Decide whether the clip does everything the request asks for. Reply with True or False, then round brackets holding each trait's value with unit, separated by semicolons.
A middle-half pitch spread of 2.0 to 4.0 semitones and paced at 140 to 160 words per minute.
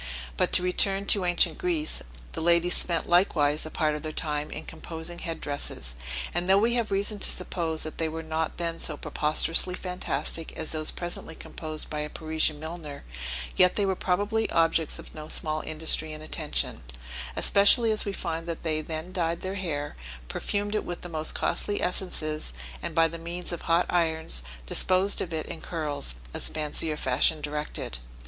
False (2.7 semitones; 185 wpm)